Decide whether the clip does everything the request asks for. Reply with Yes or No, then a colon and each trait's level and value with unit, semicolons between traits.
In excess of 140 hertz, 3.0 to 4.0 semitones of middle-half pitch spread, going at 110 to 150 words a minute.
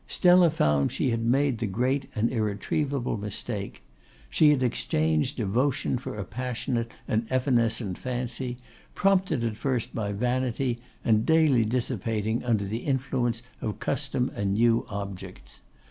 No: low, 120 Hz; average, 3.4 semitones; slow, 135 wpm